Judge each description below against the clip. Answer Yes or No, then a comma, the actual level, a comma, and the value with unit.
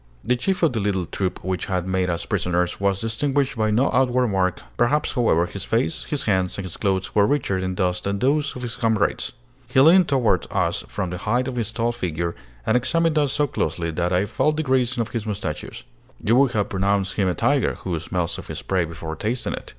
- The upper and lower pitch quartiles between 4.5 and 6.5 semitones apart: Yes, wide, 5.4 semitones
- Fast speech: Yes, fast, 225 wpm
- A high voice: No, low, 105 Hz